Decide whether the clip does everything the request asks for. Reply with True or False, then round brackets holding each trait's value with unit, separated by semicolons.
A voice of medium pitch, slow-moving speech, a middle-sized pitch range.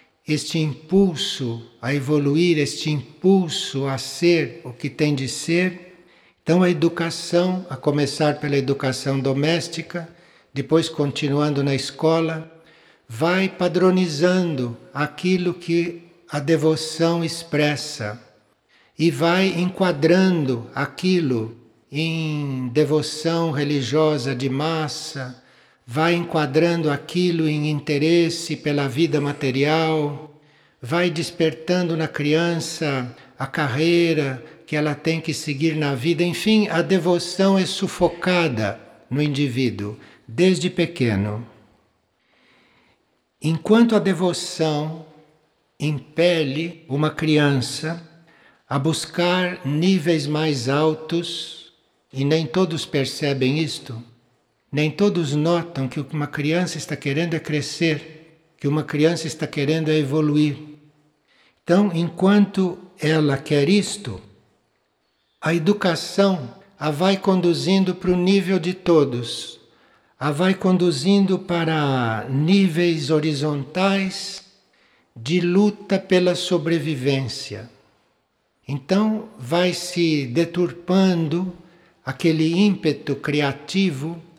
True (160 Hz; 95 wpm; 3.3 semitones)